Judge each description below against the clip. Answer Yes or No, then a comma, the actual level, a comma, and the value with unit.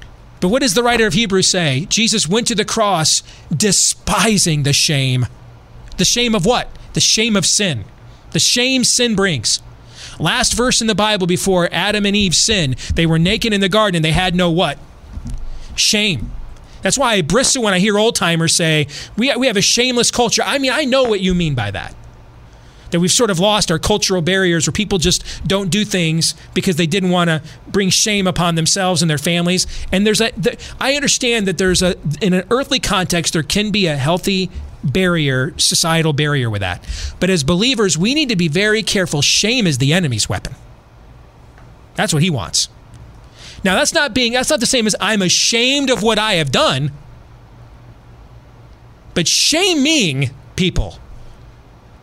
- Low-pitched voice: No, medium, 185 Hz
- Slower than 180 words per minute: No, average, 185 wpm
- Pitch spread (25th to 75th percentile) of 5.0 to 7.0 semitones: Yes, wide, 5.4 semitones